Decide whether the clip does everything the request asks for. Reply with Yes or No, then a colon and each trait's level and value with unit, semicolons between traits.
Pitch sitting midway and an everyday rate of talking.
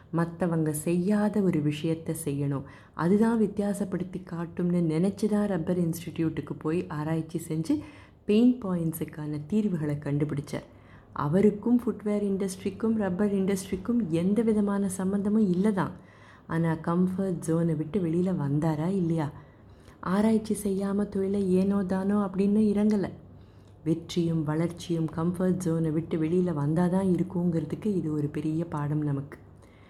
Yes: medium, 175 Hz; average, 110 wpm